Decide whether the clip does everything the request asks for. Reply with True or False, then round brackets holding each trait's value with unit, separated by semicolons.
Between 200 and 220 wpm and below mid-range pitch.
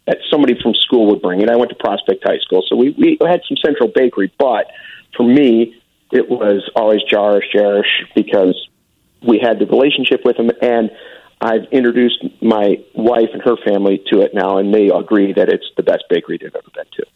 True (205 wpm; 120 Hz)